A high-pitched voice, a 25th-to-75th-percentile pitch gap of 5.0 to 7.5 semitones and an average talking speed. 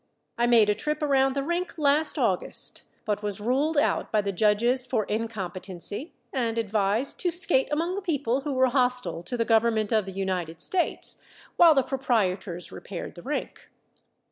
Yes: high, 235 Hz; average, 5.3 semitones; average, 170 wpm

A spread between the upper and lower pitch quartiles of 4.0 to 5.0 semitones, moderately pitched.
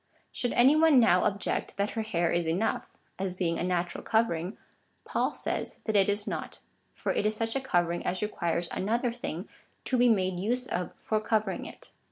No: average, 4.3 semitones; high, 205 Hz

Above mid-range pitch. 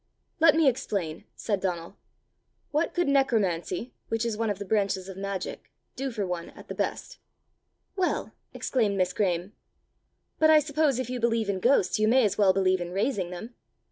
Yes: high, 210 Hz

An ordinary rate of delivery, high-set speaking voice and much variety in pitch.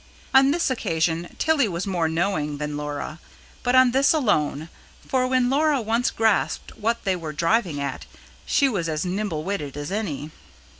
Yes: average, 165 wpm; high, 195 Hz; wide, 8.0 semitones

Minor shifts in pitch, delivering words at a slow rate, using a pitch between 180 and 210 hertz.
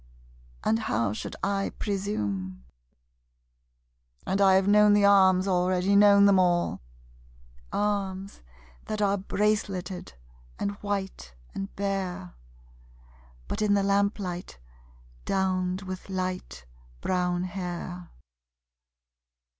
Yes: narrow, 1.9 semitones; slow, 100 wpm; high, 190 Hz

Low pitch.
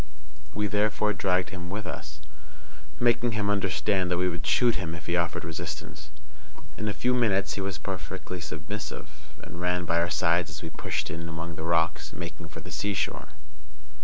Yes: very low, 90 Hz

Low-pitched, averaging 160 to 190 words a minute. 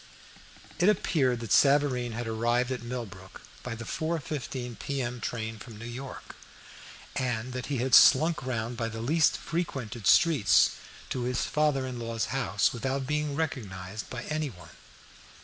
No: low, 125 Hz; average, 150 wpm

